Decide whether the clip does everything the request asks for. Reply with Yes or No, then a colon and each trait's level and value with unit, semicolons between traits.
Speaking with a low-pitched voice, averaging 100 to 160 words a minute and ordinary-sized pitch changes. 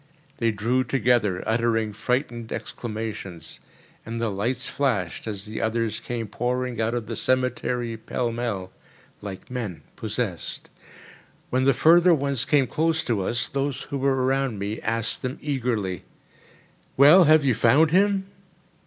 Yes: low, 120 Hz; average, 145 wpm; average, 3.4 semitones